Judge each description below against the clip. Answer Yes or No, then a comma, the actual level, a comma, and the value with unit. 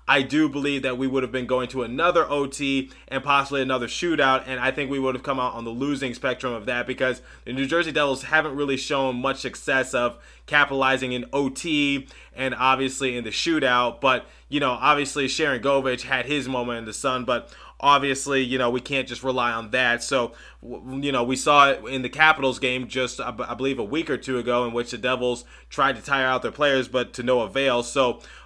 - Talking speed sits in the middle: No, fast, 220 wpm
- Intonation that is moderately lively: No, narrow, 1.7 semitones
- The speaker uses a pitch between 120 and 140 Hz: Yes, low, 130 Hz